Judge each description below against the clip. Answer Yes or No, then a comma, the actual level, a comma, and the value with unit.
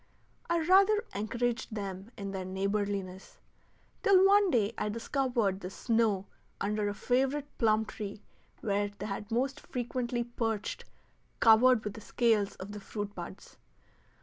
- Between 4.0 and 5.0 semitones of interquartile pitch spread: No, average, 3.6 semitones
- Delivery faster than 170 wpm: No, slow, 135 wpm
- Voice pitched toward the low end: No, high, 220 Hz